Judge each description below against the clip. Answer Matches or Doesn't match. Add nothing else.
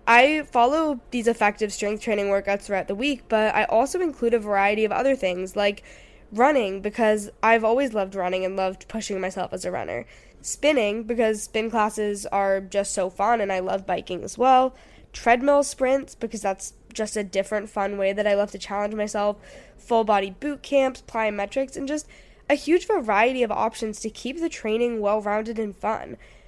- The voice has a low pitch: Doesn't match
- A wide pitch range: Doesn't match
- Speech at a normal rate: Matches